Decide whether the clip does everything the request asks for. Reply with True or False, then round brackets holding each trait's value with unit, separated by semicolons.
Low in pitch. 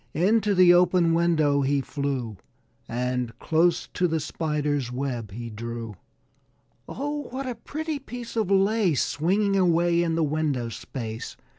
False (160 Hz)